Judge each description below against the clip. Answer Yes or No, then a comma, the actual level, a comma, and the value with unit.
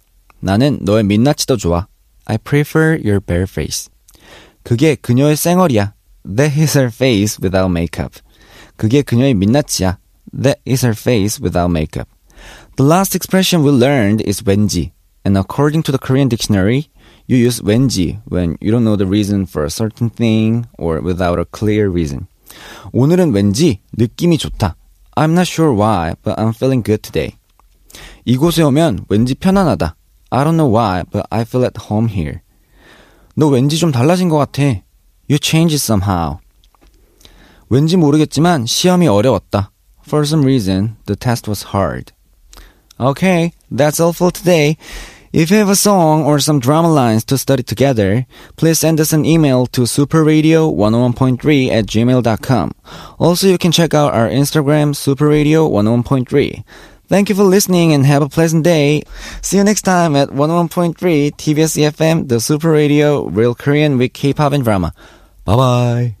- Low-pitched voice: Yes, low, 130 Hz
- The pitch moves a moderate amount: No, wide, 6.7 semitones